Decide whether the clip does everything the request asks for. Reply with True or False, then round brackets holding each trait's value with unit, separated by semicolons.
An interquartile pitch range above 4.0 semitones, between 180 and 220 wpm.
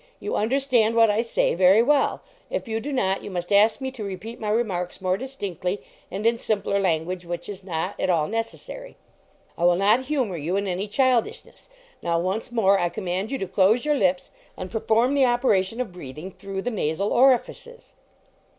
True (4.6 semitones; 190 wpm)